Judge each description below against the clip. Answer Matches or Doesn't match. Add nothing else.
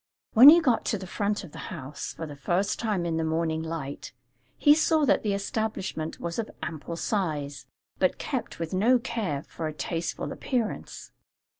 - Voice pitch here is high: Doesn't match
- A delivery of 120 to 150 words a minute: Doesn't match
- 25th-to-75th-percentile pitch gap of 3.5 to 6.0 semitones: Matches